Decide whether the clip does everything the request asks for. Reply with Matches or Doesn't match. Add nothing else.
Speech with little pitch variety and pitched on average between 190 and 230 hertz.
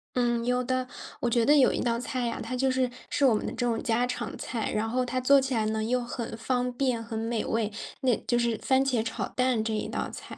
Doesn't match